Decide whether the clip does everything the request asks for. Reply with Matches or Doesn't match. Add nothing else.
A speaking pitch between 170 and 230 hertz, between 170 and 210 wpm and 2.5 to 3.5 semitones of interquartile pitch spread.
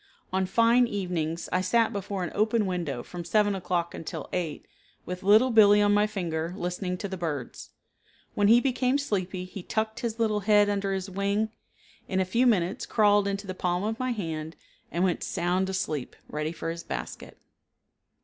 Matches